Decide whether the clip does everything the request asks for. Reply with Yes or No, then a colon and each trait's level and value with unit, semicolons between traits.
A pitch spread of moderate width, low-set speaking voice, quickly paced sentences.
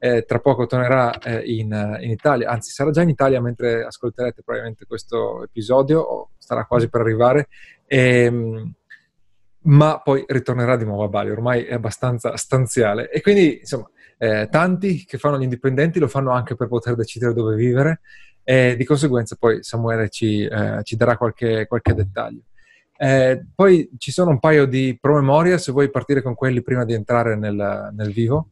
Yes: average, 3.2 semitones; low, 125 Hz; fast, 180 wpm